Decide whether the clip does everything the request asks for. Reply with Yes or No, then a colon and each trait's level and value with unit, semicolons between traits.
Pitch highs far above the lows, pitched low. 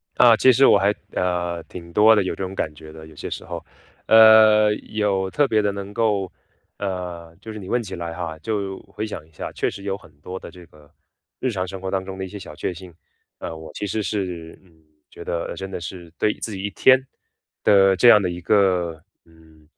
No: average, 3.5 semitones; very low, 95 Hz